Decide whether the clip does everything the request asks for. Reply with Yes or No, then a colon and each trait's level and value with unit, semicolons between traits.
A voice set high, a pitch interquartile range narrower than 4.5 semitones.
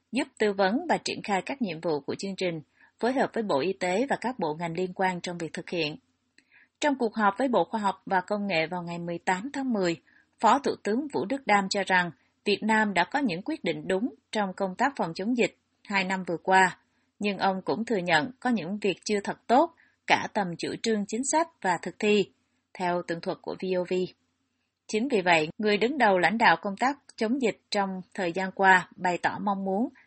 Yes: high, 195 Hz; average, 3.9 semitones